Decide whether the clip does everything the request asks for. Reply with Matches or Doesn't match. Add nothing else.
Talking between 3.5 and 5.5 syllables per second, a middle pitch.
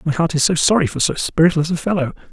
Doesn't match